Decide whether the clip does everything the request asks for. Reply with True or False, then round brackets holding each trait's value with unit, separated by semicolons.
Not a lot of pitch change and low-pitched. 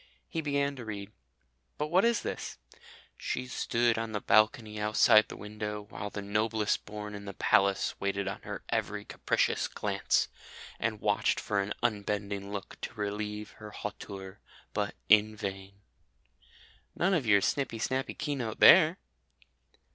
True (2.3 semitones; 105 Hz)